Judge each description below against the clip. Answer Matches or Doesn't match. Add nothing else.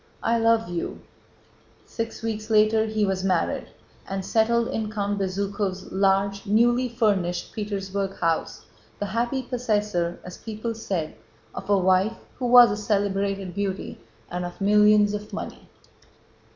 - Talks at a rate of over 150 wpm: Doesn't match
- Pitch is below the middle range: Doesn't match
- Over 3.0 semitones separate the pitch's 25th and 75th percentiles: Doesn't match